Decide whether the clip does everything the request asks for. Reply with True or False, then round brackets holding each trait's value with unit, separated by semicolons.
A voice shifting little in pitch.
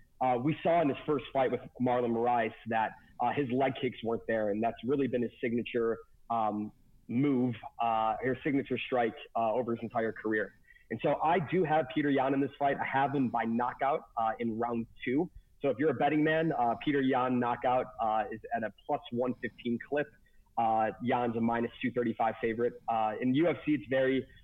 False (3.0 semitones)